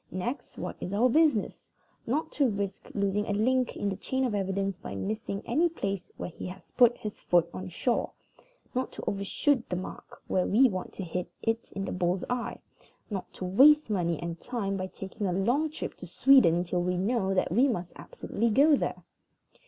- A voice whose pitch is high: Yes, high, 200 Hz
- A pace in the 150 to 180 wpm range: No, average, 200 wpm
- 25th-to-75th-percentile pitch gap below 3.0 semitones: No, average, 5.0 semitones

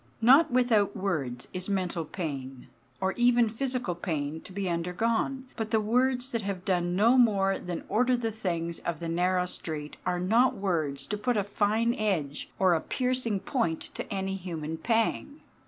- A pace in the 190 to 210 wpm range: No, average, 170 wpm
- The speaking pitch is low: No, high, 195 Hz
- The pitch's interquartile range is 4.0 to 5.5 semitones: Yes, average, 5.1 semitones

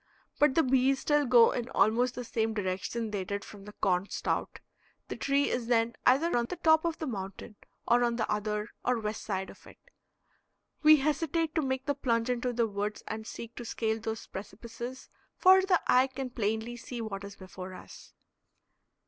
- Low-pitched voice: No, high, 235 Hz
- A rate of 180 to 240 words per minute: Yes, average, 190 wpm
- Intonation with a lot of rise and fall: No, average, 3.9 semitones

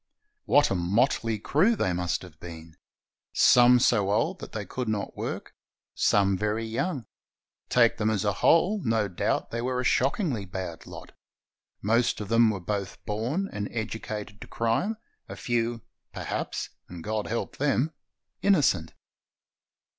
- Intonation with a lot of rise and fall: No, average, 3.7 semitones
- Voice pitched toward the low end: Yes, low, 110 Hz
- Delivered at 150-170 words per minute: Yes, average, 160 wpm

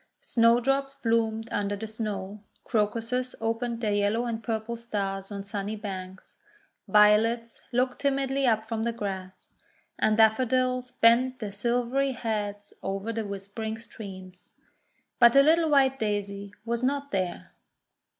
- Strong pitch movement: No, average, 3.1 semitones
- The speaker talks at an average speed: No, slow, 130 wpm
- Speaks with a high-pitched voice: Yes, high, 225 Hz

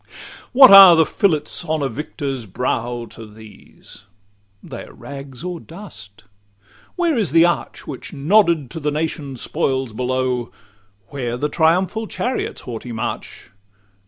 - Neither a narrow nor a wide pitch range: No, wide, 5.8 semitones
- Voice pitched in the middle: Yes, medium, 145 Hz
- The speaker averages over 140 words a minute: No, slow, 135 wpm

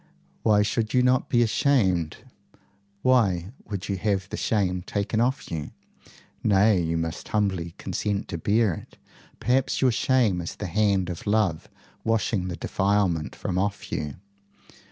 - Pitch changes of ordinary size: Yes, average, 3.8 semitones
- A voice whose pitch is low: Yes, low, 100 Hz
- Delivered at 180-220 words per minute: No, average, 150 wpm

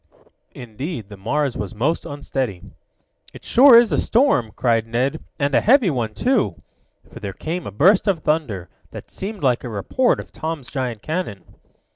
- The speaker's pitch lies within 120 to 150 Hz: Yes, medium, 140 Hz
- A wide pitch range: Yes, wide, 8.0 semitones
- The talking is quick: No, average, 170 wpm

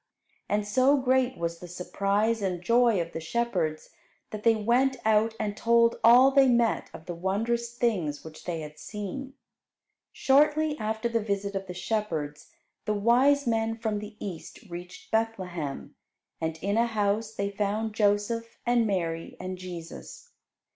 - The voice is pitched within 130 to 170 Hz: No, high, 210 Hz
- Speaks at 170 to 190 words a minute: No, average, 155 wpm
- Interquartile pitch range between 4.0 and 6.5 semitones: Yes, average, 4.4 semitones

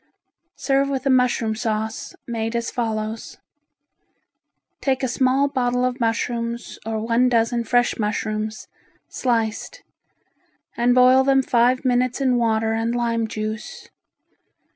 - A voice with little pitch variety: Yes, narrow, 2.2 semitones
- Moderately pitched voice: No, high, 235 Hz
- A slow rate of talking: Yes, slow, 120 wpm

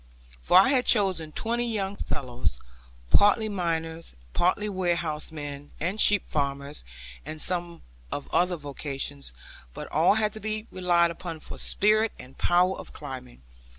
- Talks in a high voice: No, medium, 170 Hz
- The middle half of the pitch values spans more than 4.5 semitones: Yes, wide, 5.6 semitones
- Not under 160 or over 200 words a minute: No, average, 140 wpm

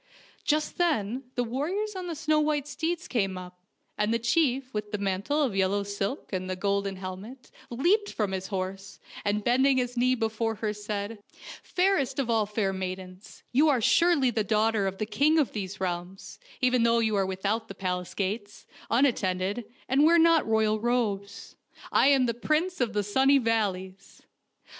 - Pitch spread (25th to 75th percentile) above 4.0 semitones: Yes, wide, 5.4 semitones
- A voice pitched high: Yes, high, 225 Hz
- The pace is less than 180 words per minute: No, average, 185 wpm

